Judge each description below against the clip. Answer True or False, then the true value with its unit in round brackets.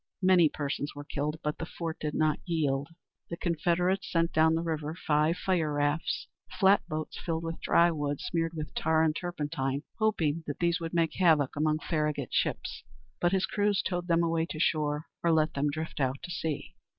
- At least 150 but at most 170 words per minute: False (190 wpm)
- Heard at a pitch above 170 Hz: False (160 Hz)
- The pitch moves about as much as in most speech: False (2.1 semitones)